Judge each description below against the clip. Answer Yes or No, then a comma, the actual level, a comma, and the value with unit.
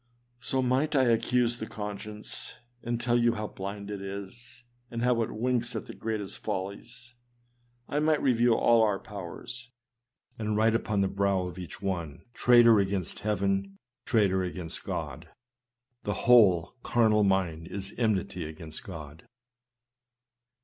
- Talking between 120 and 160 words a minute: Yes, average, 150 wpm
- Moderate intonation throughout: Yes, average, 3.7 semitones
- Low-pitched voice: Yes, low, 105 Hz